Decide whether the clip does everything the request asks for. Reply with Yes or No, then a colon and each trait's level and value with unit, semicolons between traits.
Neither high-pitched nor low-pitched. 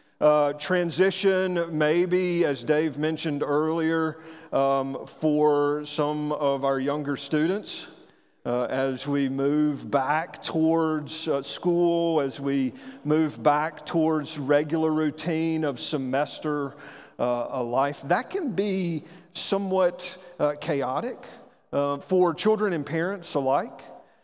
Yes: medium, 155 Hz